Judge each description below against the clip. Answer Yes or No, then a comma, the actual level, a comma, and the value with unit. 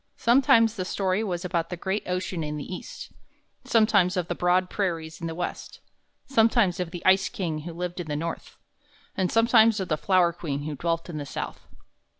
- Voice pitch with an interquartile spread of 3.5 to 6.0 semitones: No, average, 2.9 semitones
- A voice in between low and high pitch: Yes, medium, 180 Hz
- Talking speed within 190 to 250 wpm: Yes, average, 195 wpm